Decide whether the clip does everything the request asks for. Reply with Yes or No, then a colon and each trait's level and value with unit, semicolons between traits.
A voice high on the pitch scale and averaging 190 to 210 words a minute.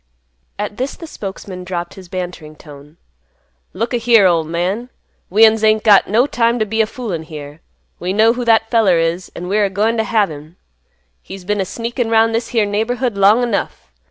Yes: high, 205 Hz; average, 195 wpm